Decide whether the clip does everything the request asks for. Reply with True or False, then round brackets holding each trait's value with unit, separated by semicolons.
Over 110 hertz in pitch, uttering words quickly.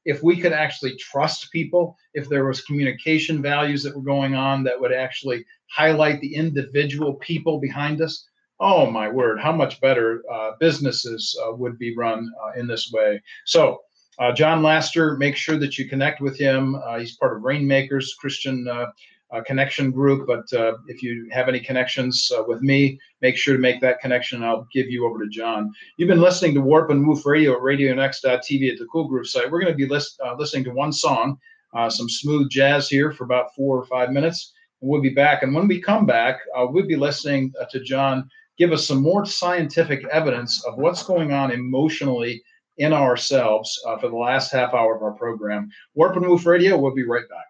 True (135 Hz; 210 wpm)